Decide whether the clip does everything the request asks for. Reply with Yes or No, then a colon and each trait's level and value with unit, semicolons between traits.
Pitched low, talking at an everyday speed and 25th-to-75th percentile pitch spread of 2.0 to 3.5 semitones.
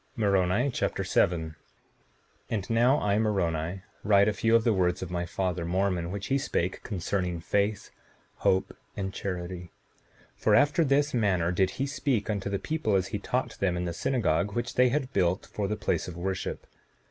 No: low, 100 Hz; average, 180 wpm; average, 4.1 semitones